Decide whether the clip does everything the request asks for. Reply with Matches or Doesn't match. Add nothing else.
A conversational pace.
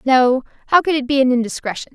Doesn't match